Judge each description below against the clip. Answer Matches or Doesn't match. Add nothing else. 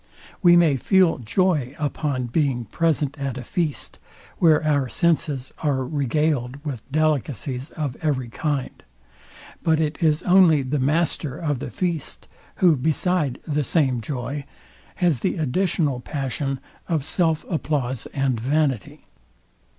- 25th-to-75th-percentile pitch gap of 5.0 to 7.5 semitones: Doesn't match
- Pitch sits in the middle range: Matches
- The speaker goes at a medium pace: Doesn't match